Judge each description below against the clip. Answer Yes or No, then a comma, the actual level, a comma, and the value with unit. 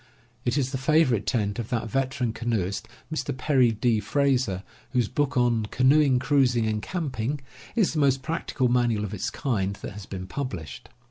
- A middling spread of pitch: Yes, average, 3.9 semitones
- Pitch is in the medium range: No, low, 125 Hz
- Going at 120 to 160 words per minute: No, average, 175 wpm